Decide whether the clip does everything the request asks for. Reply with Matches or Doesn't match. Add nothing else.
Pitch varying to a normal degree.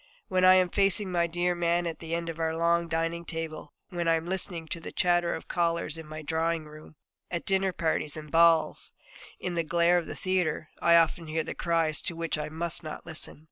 Doesn't match